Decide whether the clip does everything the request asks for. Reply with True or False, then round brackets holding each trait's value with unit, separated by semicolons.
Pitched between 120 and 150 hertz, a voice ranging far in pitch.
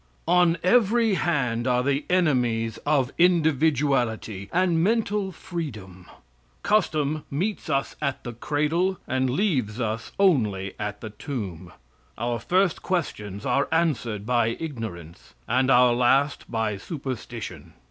True (135 Hz; 6.6 semitones)